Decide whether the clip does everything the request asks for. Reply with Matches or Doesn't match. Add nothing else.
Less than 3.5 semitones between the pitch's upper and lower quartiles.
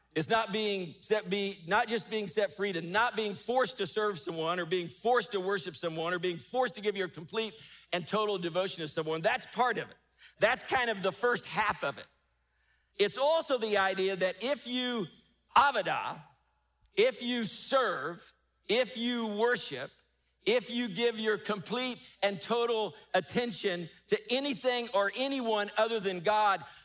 Doesn't match